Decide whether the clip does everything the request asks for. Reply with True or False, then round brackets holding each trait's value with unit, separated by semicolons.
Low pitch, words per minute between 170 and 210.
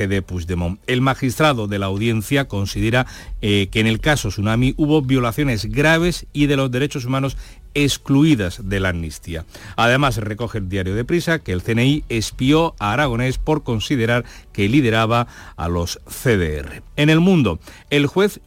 False (120 Hz; 160 wpm)